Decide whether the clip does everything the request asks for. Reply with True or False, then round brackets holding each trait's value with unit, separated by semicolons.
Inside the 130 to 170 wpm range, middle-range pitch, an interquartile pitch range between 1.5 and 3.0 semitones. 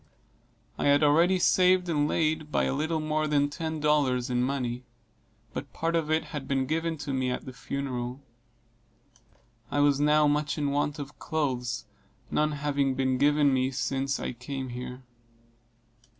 True (165 wpm; 145 Hz; 2.6 semitones)